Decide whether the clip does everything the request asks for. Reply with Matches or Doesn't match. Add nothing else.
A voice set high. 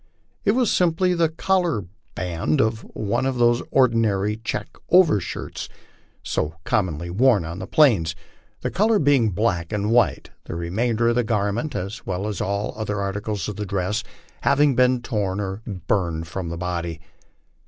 Doesn't match